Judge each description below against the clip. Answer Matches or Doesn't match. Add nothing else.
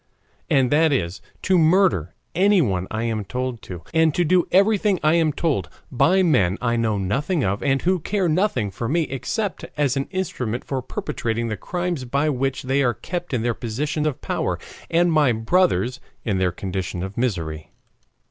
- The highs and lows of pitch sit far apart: Matches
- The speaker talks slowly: Doesn't match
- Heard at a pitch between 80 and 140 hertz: Matches